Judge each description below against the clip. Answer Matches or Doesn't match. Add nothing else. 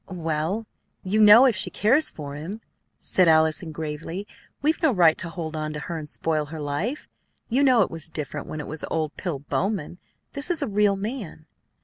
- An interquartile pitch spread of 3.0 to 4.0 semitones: Doesn't match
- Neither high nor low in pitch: Matches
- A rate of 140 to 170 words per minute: Doesn't match